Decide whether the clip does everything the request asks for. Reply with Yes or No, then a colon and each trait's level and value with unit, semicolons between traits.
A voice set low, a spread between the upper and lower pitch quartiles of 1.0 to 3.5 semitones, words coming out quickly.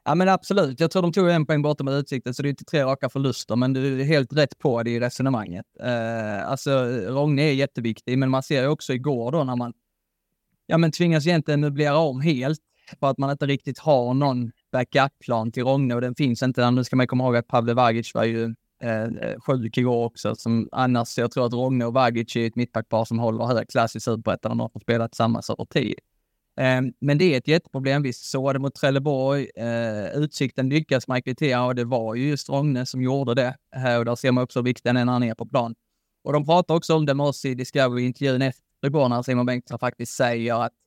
Yes: low, 130 Hz; average, 2.9 semitones; fast, 225 wpm